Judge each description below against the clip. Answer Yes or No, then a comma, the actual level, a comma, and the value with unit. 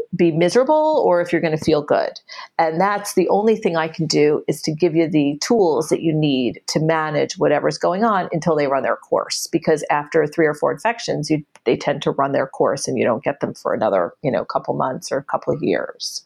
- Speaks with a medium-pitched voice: Yes, medium, 165 Hz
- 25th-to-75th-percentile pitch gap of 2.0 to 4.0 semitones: Yes, average, 2.8 semitones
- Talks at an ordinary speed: No, fast, 240 wpm